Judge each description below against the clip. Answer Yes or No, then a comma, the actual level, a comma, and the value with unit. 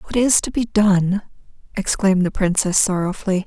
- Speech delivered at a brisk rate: No, average, 155 wpm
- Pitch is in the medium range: No, high, 195 Hz